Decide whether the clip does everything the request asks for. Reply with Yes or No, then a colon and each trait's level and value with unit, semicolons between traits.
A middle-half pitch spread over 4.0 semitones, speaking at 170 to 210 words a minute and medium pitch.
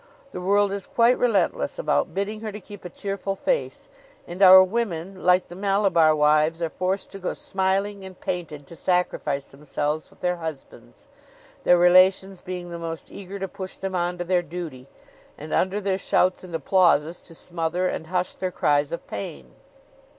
No: average, 2.9 semitones; average, 180 wpm; medium, 180 Hz